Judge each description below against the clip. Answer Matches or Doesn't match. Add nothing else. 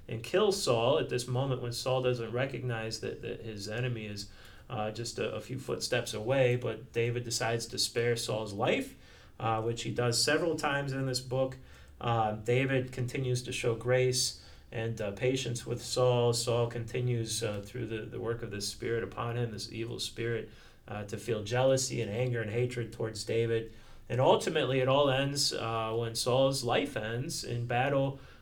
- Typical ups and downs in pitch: Doesn't match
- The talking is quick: Doesn't match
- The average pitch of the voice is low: Matches